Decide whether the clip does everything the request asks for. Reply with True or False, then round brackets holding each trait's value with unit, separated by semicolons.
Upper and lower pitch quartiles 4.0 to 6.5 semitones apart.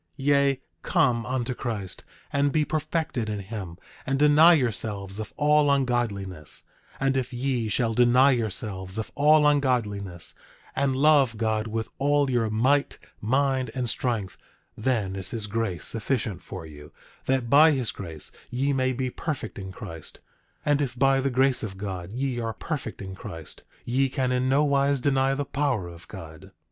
True (4.7 semitones)